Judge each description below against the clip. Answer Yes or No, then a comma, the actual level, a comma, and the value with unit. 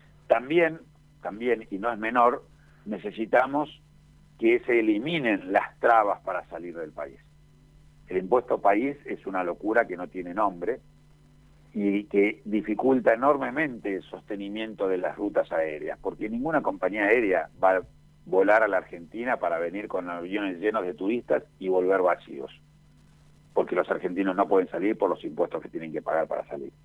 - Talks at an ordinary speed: Yes, average, 160 wpm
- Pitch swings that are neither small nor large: No, wide, 8.3 semitones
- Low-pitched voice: Yes, low, 110 Hz